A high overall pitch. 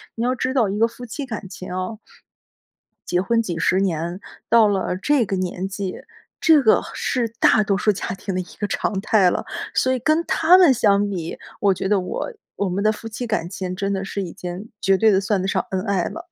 Yes: high, 200 Hz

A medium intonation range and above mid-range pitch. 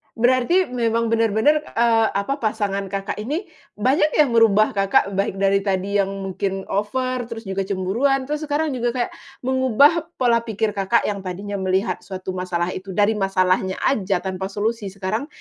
Yes: average, 4.1 semitones; high, 210 Hz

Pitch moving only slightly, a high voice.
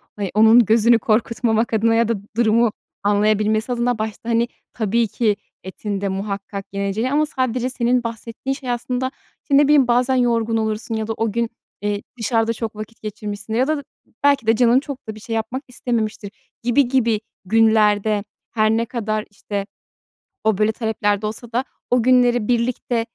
Yes: narrow, 2.2 semitones; high, 225 Hz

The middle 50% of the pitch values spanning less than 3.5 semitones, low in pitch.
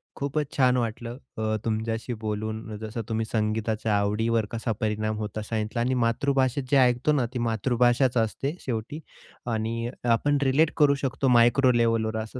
Yes: narrow, 2.6 semitones; low, 115 Hz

